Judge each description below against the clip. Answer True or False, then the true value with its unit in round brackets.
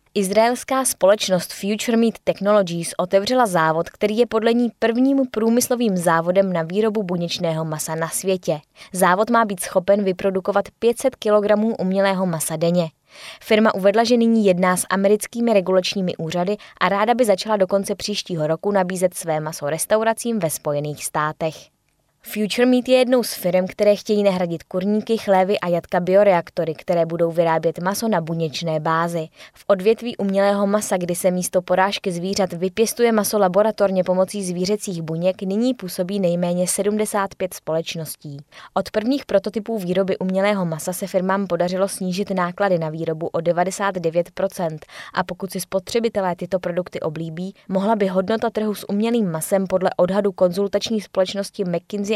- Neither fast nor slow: True (150 wpm)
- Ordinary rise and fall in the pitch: True (3.2 semitones)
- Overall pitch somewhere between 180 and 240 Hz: True (190 Hz)